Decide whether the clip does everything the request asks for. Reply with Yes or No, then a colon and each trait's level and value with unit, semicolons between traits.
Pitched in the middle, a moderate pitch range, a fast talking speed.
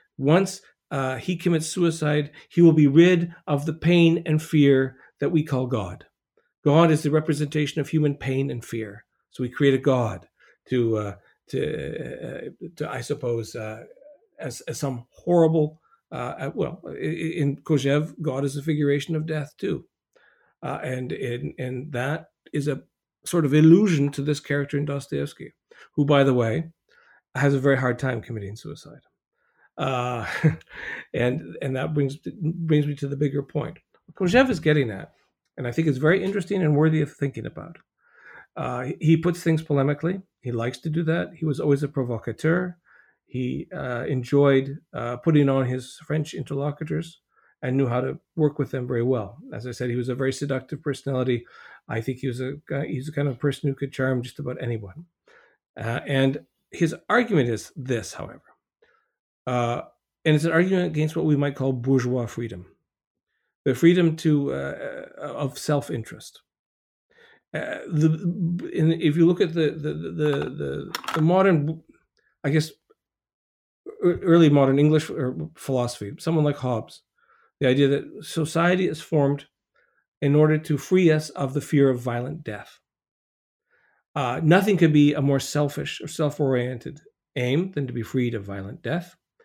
No: medium, 145 Hz; average, 3.6 semitones; average, 165 wpm